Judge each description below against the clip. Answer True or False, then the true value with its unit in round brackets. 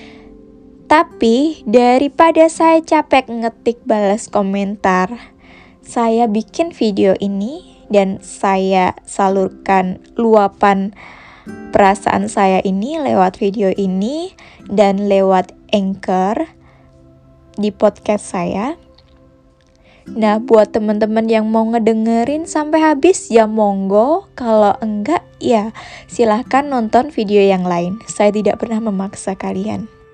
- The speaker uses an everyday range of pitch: True (3.3 semitones)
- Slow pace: False (100 wpm)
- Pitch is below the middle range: False (210 Hz)